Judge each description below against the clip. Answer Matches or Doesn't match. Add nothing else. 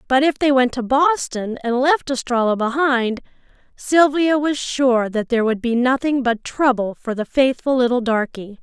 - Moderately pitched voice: Doesn't match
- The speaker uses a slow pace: Doesn't match